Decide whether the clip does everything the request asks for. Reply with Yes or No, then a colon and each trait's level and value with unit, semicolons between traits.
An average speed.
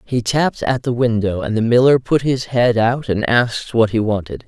No: fast, 230 wpm